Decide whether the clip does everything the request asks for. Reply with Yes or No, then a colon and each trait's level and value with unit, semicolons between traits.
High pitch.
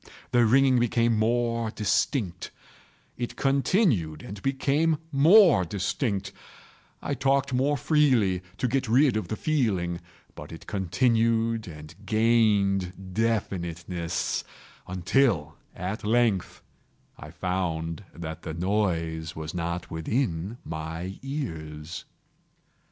No: low, 105 Hz